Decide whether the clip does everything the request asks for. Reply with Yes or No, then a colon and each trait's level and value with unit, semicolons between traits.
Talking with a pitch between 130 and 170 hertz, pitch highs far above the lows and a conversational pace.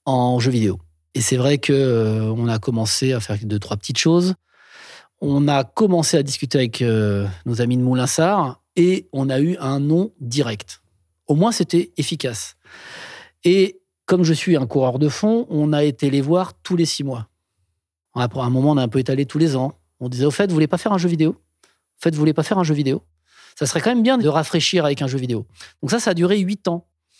No: medium, 140 Hz; wide, 5.9 semitones; fast, 230 wpm